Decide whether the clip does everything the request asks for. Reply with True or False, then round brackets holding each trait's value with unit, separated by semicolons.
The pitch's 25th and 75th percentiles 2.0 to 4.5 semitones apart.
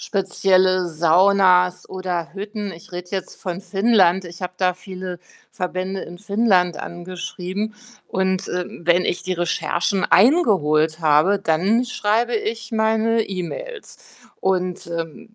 True (2.6 semitones)